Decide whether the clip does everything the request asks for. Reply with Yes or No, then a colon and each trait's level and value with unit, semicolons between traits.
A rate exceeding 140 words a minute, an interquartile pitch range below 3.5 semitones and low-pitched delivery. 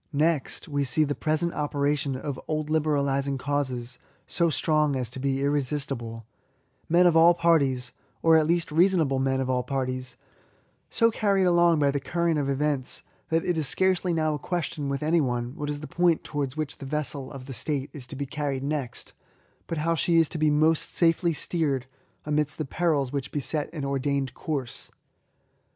No: average, 190 wpm; average, 3.0 semitones; medium, 145 Hz